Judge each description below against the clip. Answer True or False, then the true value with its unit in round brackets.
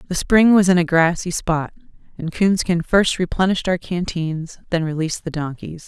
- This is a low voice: False (175 Hz)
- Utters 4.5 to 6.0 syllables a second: True (5.1 syllables/s)